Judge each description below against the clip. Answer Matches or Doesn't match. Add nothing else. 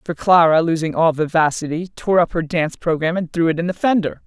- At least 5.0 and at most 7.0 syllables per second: Matches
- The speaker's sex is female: Matches